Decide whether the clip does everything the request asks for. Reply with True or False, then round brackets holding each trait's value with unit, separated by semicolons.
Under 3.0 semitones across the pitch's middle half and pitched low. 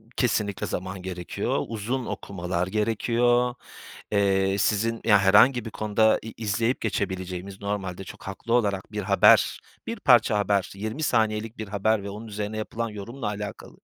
True (2.5 semitones; 105 Hz)